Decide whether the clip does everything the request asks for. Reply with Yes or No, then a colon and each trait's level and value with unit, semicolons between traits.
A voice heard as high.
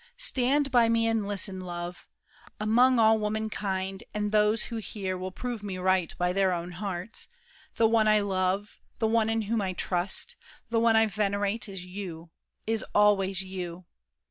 Yes: high, 205 Hz